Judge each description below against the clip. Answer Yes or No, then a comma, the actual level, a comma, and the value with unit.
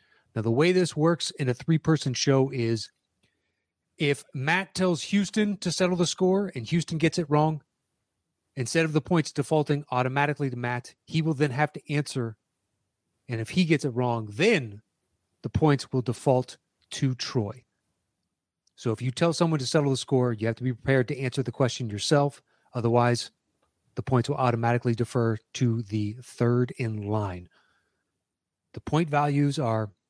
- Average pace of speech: Yes, average, 170 wpm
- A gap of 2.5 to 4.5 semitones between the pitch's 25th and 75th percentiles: No, average, 5.2 semitones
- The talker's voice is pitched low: Yes, low, 130 Hz